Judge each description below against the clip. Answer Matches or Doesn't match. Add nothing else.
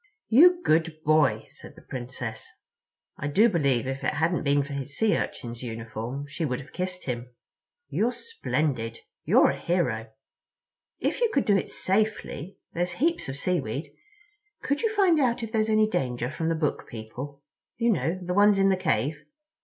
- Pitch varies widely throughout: Matches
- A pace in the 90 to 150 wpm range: Doesn't match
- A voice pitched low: Doesn't match